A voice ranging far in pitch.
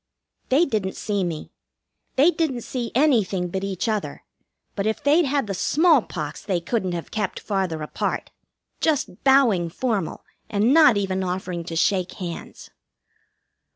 Yes: wide, 6.5 semitones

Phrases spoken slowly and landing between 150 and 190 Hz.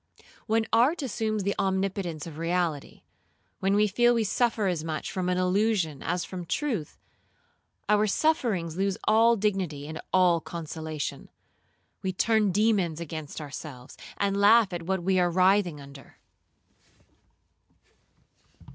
Yes: slow, 130 wpm; medium, 185 Hz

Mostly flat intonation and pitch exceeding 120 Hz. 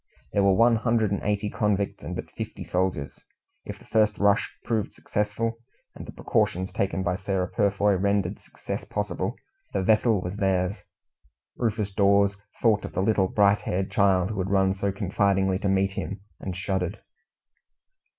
No: narrow, 1.7 semitones; low, 100 Hz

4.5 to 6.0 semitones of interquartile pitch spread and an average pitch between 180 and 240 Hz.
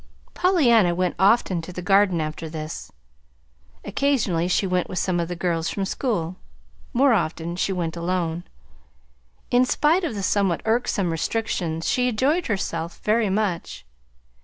Yes: average, 5.0 semitones; medium, 185 Hz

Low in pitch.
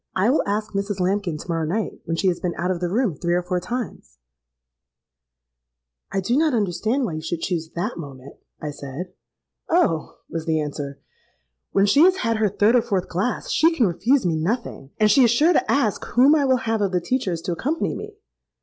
No: medium, 185 Hz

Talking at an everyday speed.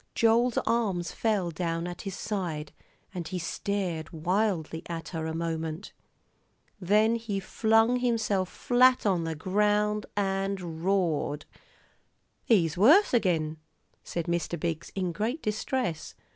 No: slow, 125 wpm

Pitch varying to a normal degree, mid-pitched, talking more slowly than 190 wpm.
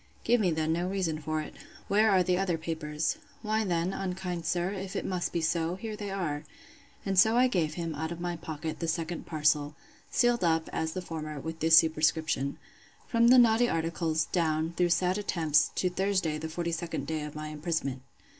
No: average, 3.0 semitones; medium, 170 Hz; average, 195 wpm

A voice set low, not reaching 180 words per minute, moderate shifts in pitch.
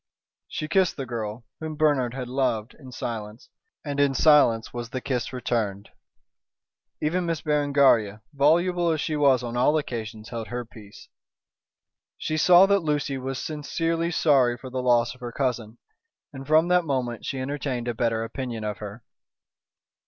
Yes: low, 130 Hz; average, 160 wpm; average, 4.2 semitones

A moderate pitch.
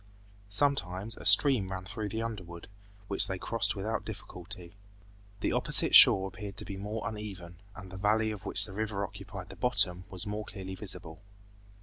No: low, 100 Hz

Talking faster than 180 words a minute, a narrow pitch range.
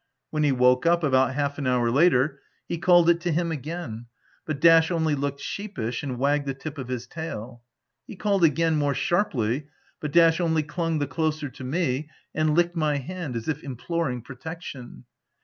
No: average, 190 wpm; average, 4.3 semitones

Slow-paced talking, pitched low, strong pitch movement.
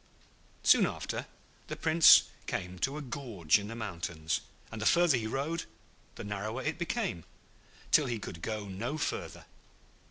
No: average, 155 wpm; low, 115 Hz; wide, 7.2 semitones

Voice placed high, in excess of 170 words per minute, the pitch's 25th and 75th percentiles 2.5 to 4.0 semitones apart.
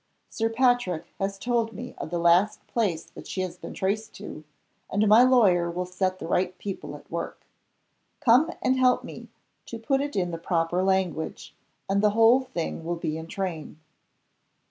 No: high, 195 Hz; average, 180 wpm; average, 4.8 semitones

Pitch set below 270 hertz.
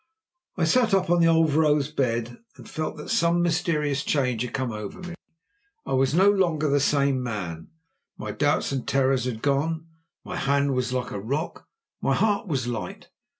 Yes: medium, 140 Hz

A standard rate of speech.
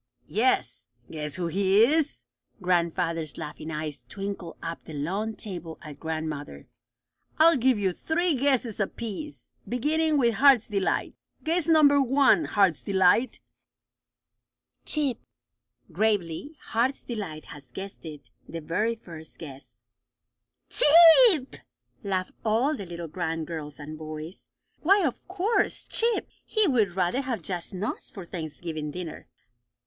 No: slow, 125 wpm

